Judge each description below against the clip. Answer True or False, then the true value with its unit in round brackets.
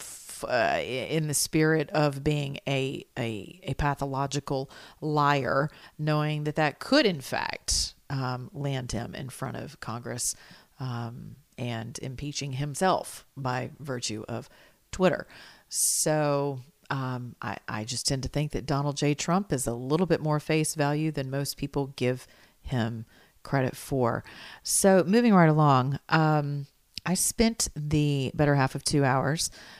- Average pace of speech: True (145 wpm)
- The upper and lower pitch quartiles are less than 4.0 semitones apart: True (2.9 semitones)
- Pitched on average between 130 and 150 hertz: True (140 Hz)